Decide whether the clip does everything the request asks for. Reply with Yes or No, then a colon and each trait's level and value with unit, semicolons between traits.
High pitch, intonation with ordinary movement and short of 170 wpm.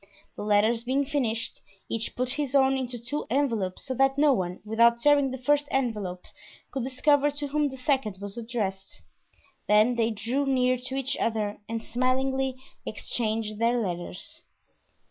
Yes: high, 245 Hz; average, 3.6 semitones; average, 160 wpm